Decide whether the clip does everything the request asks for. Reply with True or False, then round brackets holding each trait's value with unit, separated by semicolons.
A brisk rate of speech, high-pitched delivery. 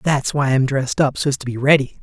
False (325 wpm; 135 Hz)